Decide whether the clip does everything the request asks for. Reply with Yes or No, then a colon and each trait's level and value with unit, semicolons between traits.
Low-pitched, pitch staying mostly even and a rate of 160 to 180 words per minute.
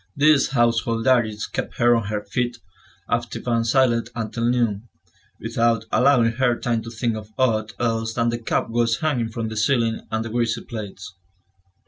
Yes: low, 115 Hz; narrow, 1.3 semitones; average, 165 wpm